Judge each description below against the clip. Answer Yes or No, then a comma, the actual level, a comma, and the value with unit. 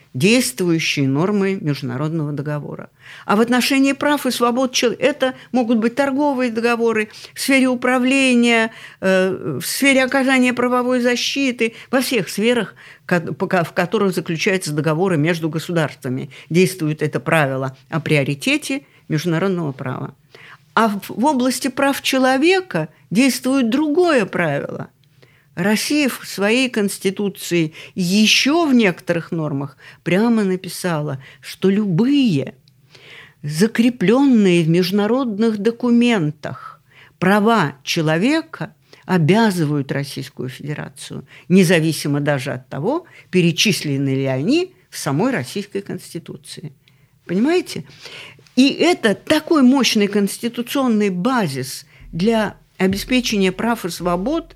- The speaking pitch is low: No, high, 195 Hz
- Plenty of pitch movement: Yes, wide, 7.9 semitones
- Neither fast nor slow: No, slow, 100 wpm